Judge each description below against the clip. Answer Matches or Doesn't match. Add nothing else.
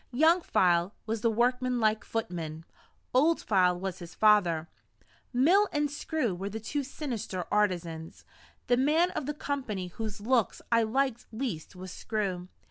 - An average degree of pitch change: Doesn't match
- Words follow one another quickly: Doesn't match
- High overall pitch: Matches